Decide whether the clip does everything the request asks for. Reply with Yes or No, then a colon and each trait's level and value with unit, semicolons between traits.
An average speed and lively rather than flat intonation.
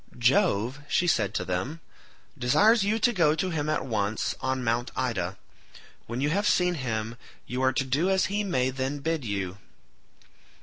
Yes: average, 175 wpm; wide, 6.6 semitones